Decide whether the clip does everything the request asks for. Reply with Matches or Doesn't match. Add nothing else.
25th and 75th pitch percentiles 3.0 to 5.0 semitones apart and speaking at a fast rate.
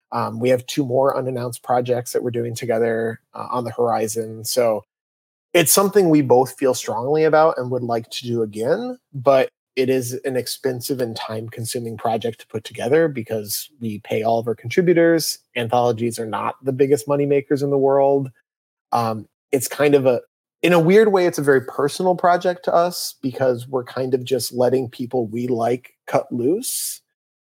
Doesn't match